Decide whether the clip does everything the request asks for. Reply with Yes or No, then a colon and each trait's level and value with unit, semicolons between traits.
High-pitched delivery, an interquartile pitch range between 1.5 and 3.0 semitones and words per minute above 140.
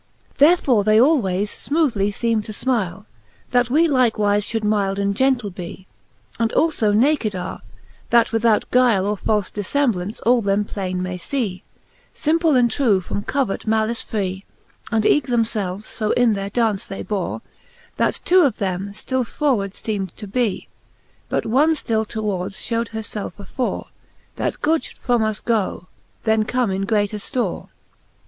No: high, 220 Hz; average, 3.7 semitones; average, 160 wpm